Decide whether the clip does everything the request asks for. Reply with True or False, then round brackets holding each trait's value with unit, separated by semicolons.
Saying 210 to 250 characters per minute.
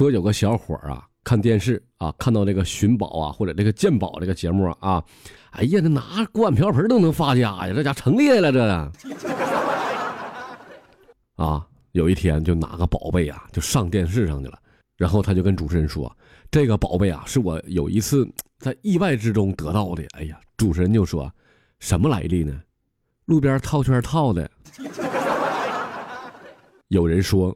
True (245 characters per minute)